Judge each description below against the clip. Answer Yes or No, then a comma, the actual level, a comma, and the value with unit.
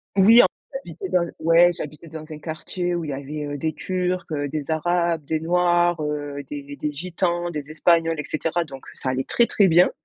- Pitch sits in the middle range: Yes, medium, 160 Hz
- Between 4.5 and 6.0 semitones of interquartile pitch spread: No, average, 2.7 semitones